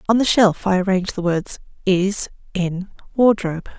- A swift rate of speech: No, average, 160 wpm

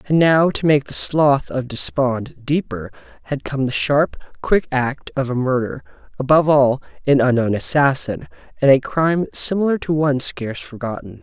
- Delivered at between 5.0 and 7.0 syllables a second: Yes, 5.1 syllables/s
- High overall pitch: No, low, 130 Hz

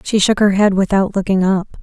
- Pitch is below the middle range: No, high, 195 Hz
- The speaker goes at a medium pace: No, fast, 230 wpm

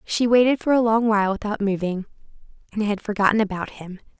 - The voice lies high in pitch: Yes, high, 210 Hz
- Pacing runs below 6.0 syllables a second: No, 6.2 syllables/s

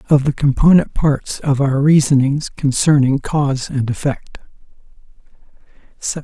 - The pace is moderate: No, slow, 115 wpm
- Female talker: No, male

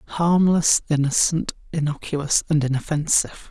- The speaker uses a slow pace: Yes, slow, 85 wpm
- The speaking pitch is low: No, medium, 155 Hz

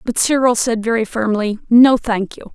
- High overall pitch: Yes, high, 230 Hz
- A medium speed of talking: Yes, average, 190 wpm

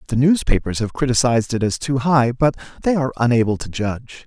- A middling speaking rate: Yes, average, 195 wpm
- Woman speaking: No, male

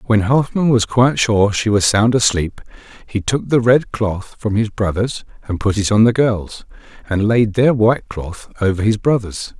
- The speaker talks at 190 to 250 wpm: Yes, average, 195 wpm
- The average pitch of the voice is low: Yes, low, 110 Hz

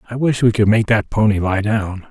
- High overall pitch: No, low, 110 Hz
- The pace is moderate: No, fast, 255 wpm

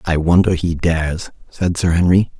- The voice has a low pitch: Yes, very low, 85 Hz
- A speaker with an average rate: Yes, average, 175 wpm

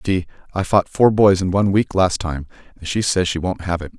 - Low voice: Yes, very low, 95 Hz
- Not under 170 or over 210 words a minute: No, fast, 270 wpm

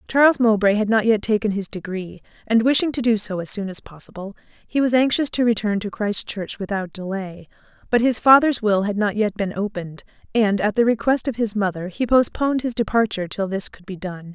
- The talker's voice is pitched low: No, high, 210 Hz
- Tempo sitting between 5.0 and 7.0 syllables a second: Yes, 5.6 syllables/s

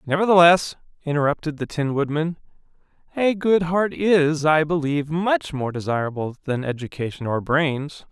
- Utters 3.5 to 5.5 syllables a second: Yes, 4.9 syllables/s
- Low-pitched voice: No, medium, 155 Hz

